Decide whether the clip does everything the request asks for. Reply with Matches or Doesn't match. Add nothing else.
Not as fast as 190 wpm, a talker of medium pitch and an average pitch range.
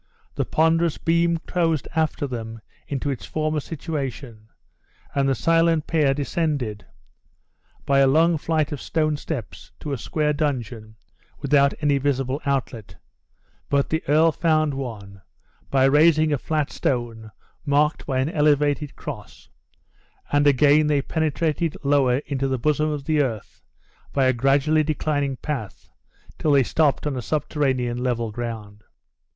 Matches